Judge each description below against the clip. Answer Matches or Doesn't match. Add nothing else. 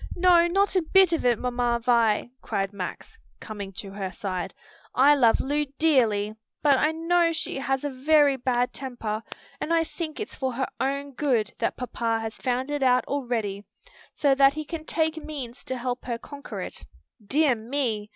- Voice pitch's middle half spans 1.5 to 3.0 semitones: Doesn't match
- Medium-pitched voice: Doesn't match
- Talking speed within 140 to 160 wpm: Doesn't match